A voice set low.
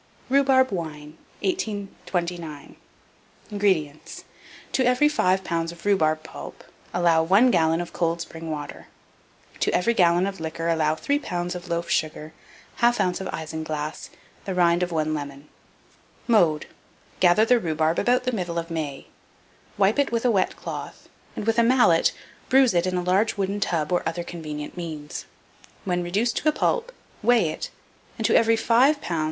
No: medium, 175 Hz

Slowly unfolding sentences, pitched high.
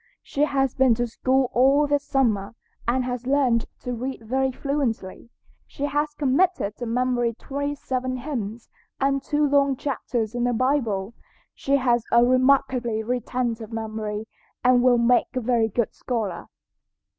No: average, 150 wpm; very high, 250 Hz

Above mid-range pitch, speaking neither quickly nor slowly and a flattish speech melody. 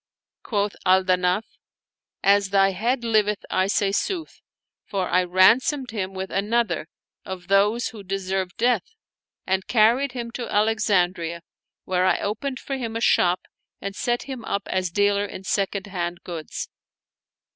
No: high, 200 Hz; average, 150 wpm; average, 3.4 semitones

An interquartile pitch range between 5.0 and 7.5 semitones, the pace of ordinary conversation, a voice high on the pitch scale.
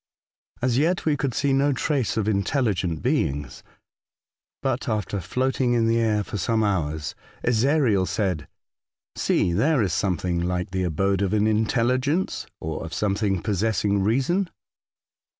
No: wide, 5.5 semitones; average, 145 wpm; low, 105 Hz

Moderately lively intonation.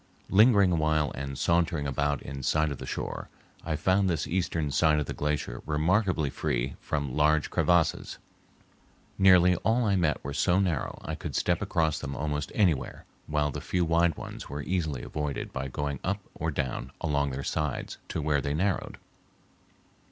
Yes: average, 3.5 semitones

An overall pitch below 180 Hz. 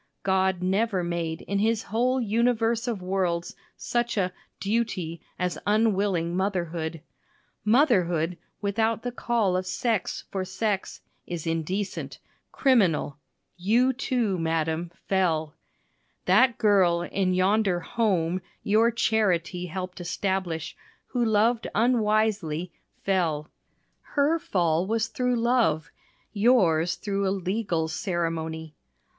No: high, 190 Hz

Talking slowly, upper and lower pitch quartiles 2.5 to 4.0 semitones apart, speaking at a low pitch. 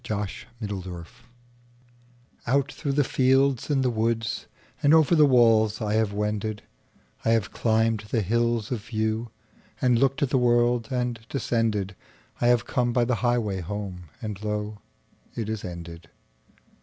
Yes: slow, 130 wpm; average, 2.8 semitones; low, 115 Hz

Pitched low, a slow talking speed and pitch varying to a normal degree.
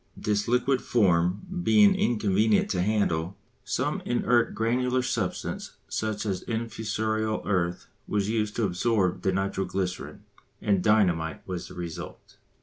Yes: low, 105 Hz; slow, 130 wpm; average, 3.7 semitones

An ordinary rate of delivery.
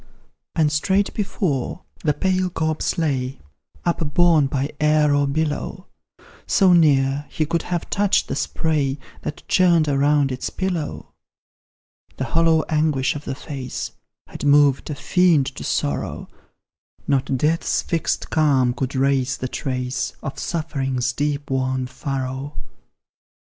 No: slow, 130 wpm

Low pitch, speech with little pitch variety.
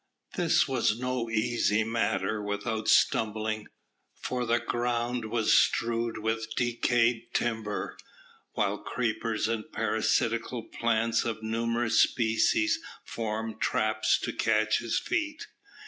Yes: low, 115 Hz; narrow, 1.5 semitones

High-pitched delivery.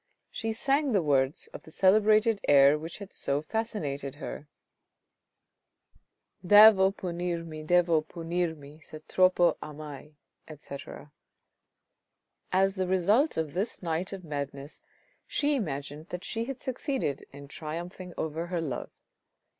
No: medium, 170 Hz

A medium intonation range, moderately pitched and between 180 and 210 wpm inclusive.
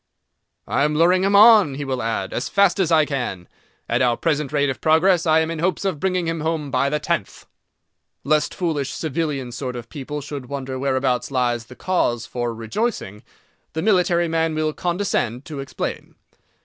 Yes: average, 4.6 semitones; medium, 150 Hz; average, 185 wpm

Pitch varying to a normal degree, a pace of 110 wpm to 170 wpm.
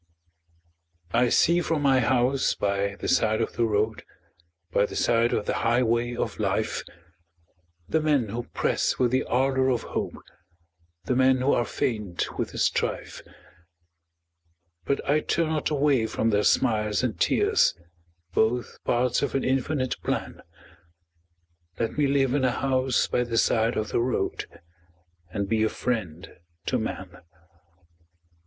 Yes: average, 3.2 semitones; average, 150 wpm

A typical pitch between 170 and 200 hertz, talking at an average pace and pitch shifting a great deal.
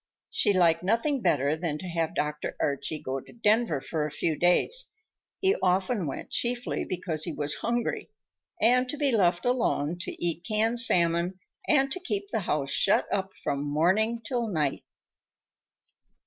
Yes: medium, 185 Hz; average, 155 wpm; wide, 7.0 semitones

